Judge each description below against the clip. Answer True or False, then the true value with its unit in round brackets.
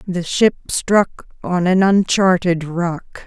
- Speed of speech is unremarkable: False (130 wpm)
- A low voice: False (180 Hz)